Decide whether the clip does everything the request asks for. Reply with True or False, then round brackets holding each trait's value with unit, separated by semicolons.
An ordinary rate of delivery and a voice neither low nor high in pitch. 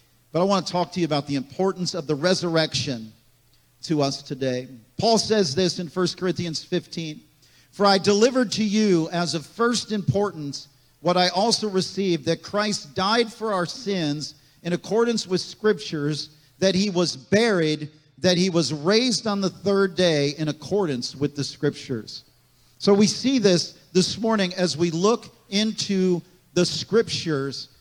True (160 wpm; 175 Hz)